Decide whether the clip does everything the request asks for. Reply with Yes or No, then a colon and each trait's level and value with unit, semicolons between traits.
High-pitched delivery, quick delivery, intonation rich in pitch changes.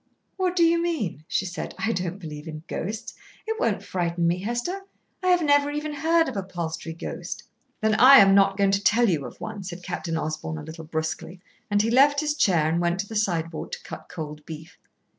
Yes: high, 195 Hz; fast, 215 wpm; wide, 8.5 semitones